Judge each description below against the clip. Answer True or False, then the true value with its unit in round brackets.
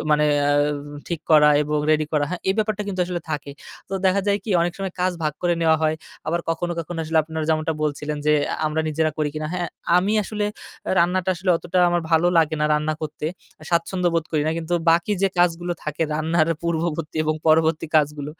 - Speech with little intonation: True (2.3 semitones)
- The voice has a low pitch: False (160 Hz)